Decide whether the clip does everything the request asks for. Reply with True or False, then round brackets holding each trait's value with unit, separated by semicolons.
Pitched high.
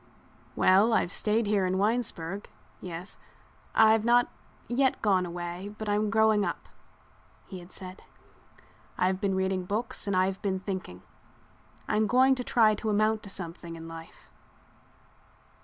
True (200 Hz)